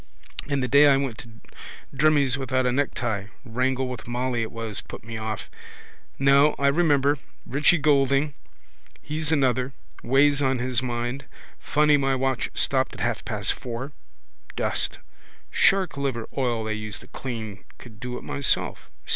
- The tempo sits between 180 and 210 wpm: No, average, 155 wpm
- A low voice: Yes, low, 130 Hz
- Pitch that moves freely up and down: No, average, 2.8 semitones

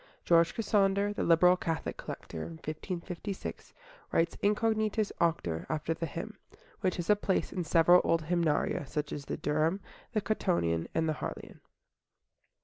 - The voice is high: No, medium, 170 Hz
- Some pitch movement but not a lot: Yes, average, 3.7 semitones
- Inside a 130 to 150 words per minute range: Yes, average, 140 wpm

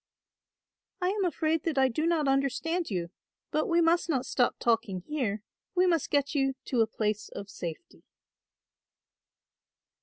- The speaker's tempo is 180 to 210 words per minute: No, average, 150 wpm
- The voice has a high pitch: Yes, very high, 275 Hz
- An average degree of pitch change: No, wide, 6.5 semitones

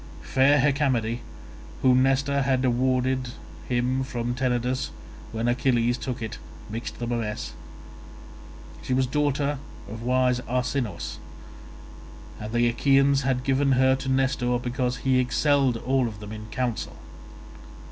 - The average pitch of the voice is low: Yes, low, 125 Hz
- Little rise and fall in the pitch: Yes, narrow, 1.7 semitones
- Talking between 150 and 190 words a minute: No, slow, 135 wpm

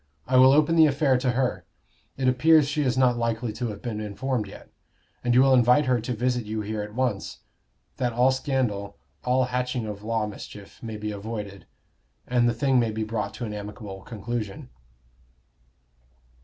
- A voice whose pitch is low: Yes, low, 120 Hz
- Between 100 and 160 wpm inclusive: No, average, 185 wpm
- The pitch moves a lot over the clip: No, average, 3.3 semitones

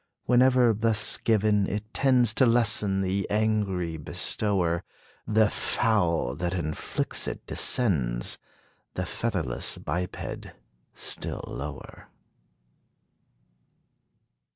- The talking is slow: Yes, slow, 85 wpm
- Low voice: Yes, low, 100 Hz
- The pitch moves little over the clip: No, average, 4.6 semitones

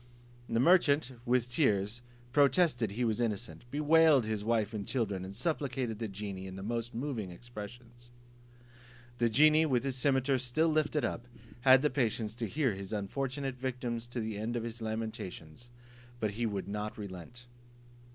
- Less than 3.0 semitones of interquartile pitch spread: No, average, 3.7 semitones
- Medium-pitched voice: No, low, 120 Hz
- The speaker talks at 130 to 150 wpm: No, average, 160 wpm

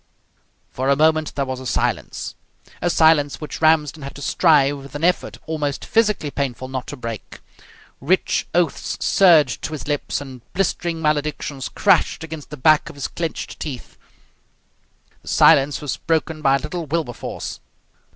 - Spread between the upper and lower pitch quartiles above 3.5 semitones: No, average, 2.7 semitones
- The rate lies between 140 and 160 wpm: Yes, average, 155 wpm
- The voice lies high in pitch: No, medium, 150 Hz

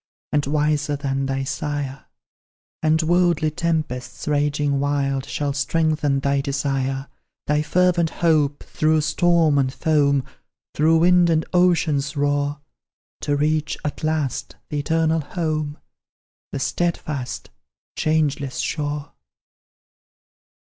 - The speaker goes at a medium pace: No, slow, 105 wpm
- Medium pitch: Yes, medium, 150 Hz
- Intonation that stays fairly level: Yes, narrow, 2.0 semitones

